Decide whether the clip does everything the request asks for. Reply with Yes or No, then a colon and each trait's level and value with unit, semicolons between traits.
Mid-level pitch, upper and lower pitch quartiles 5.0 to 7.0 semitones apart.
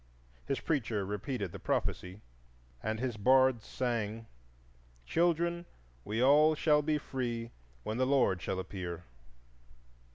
No: low, 120 Hz; average, 5.3 semitones